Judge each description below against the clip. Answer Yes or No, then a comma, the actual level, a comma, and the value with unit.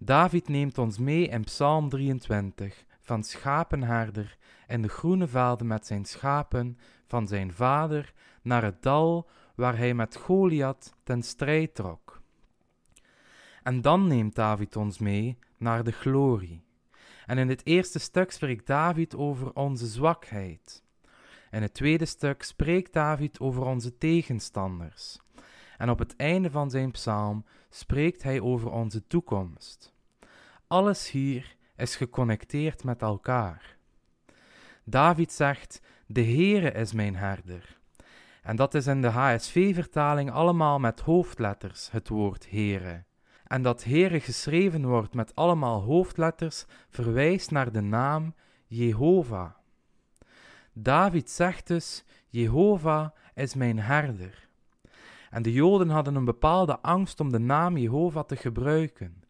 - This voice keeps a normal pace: No, slow, 130 wpm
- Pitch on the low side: Yes, low, 130 Hz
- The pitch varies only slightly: No, wide, 5.5 semitones